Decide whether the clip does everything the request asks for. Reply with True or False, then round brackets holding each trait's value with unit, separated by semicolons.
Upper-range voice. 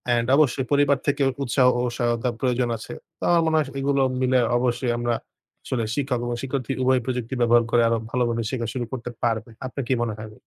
False (125 Hz)